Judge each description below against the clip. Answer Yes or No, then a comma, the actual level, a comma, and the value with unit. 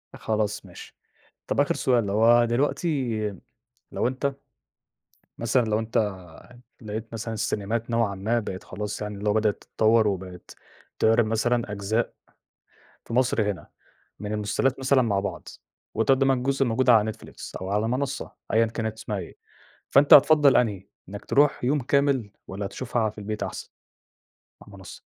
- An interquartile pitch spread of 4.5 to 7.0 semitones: No, average, 3.3 semitones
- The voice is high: No, low, 110 Hz